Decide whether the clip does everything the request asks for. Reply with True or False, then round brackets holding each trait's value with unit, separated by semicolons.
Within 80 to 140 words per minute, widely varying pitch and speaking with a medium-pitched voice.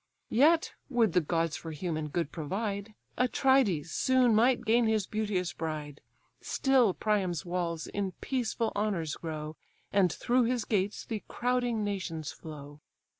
False (135 wpm; 6.1 semitones; 200 Hz)